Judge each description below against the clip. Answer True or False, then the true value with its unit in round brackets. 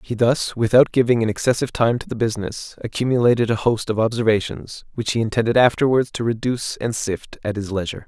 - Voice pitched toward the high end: False (115 Hz)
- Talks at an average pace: True (195 wpm)